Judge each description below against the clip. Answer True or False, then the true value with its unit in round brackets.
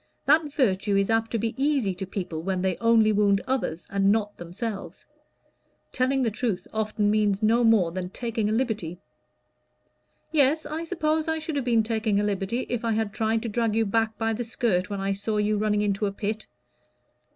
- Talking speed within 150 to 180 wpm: False (195 wpm)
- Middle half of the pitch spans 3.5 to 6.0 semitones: False (2.9 semitones)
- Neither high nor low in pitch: False (220 Hz)